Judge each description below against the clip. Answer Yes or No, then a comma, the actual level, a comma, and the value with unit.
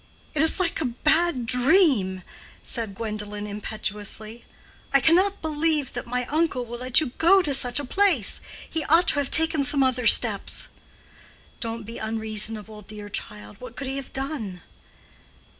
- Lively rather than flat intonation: Yes, wide, 6.2 semitones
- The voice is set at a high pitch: Yes, very high, 250 Hz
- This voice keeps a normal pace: Yes, average, 160 wpm